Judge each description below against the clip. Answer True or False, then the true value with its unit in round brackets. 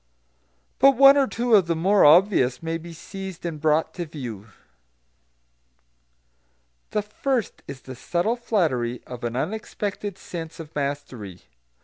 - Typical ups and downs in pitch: False (6.8 semitones)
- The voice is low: False (165 Hz)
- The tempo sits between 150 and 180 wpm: False (135 wpm)